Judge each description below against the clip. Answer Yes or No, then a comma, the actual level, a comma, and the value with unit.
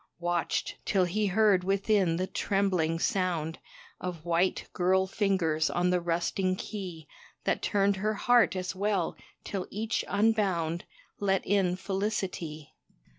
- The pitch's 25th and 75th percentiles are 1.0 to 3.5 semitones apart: Yes, narrow, 2.6 semitones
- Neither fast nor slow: No, slow, 125 wpm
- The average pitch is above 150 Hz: Yes, medium, 185 Hz